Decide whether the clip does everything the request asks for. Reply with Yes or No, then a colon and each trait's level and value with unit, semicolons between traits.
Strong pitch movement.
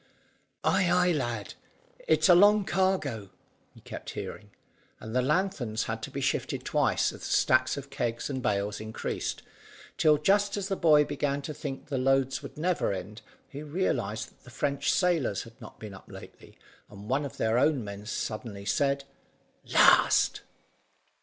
Yes: wide, 5.7 semitones